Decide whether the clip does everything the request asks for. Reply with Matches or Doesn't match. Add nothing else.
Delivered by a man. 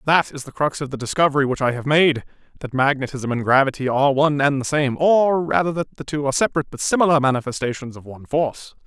Matches